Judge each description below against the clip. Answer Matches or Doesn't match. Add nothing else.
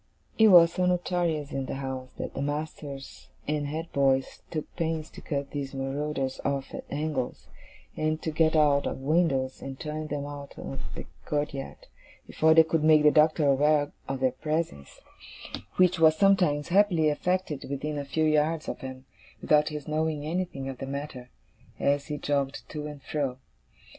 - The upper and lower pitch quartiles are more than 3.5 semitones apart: Doesn't match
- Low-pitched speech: Doesn't match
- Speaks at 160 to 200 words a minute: Matches